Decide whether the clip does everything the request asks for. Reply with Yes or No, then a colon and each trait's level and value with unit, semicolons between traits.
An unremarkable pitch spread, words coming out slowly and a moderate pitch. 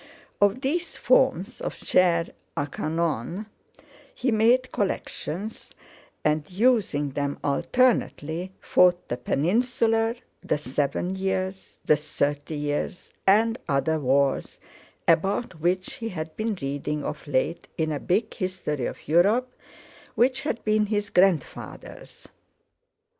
No: wide, 6.6 semitones; slow, 115 wpm; medium, 180 Hz